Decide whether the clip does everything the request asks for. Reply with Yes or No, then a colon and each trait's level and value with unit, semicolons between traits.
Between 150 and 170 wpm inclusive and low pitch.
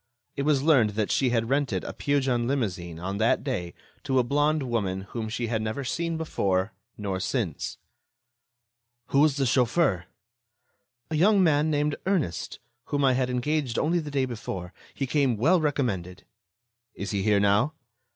Yes: average, 165 wpm; low, 125 Hz